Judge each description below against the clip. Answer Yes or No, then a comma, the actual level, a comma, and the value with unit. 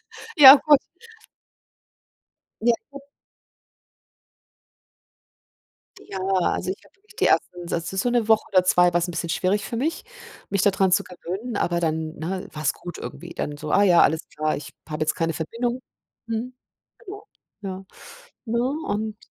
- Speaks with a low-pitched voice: No, high, 190 Hz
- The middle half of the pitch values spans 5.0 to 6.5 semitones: Yes, wide, 5.4 semitones